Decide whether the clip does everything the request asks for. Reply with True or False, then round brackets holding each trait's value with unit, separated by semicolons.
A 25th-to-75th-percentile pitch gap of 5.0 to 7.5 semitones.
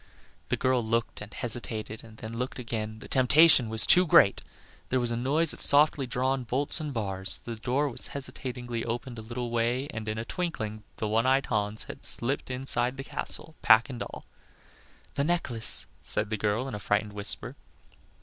False (3.3 semitones)